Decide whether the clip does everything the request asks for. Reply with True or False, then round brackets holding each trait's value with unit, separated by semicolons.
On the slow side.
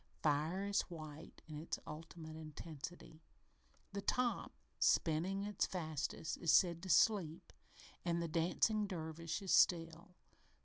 True (125 wpm)